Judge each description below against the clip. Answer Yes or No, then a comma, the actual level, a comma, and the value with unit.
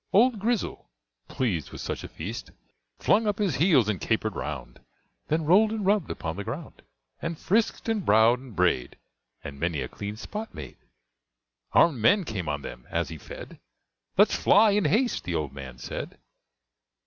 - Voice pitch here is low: Yes, low, 125 Hz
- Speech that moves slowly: No, average, 170 wpm